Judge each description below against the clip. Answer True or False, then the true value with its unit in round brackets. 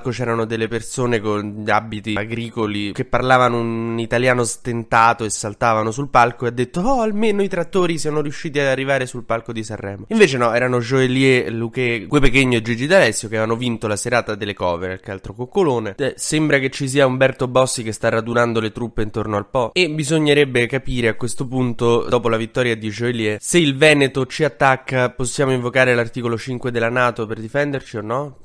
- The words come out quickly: True (190 wpm)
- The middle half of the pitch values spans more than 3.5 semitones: False (2.8 semitones)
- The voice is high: False (120 Hz)